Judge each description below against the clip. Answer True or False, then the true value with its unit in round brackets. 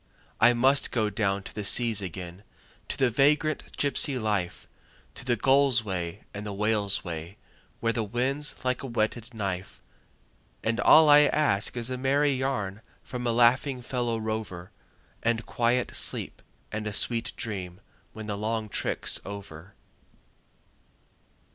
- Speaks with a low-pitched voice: True (115 Hz)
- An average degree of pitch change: True (4.0 semitones)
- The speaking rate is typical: True (150 wpm)